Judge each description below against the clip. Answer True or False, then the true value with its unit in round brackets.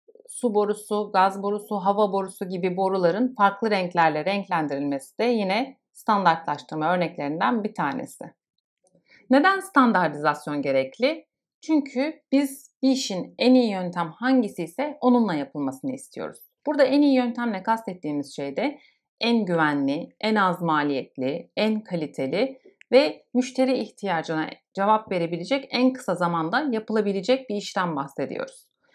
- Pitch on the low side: False (210 Hz)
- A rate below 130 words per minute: True (120 wpm)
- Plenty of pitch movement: True (7.2 semitones)